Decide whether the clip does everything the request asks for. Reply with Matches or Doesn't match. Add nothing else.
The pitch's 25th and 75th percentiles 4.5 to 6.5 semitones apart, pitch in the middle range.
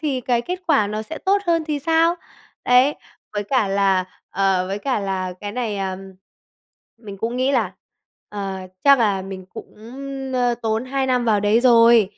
Doesn't match